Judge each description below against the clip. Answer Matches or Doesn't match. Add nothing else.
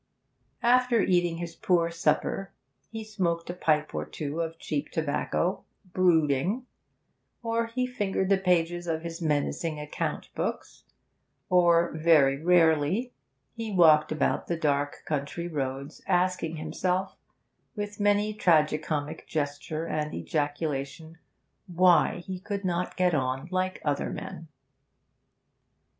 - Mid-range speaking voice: Matches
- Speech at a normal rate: Doesn't match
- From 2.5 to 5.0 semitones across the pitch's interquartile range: Matches